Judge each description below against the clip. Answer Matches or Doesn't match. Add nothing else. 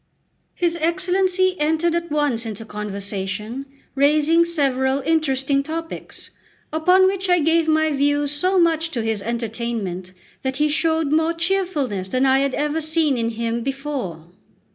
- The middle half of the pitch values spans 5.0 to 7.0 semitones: Matches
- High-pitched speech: Matches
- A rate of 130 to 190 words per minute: Matches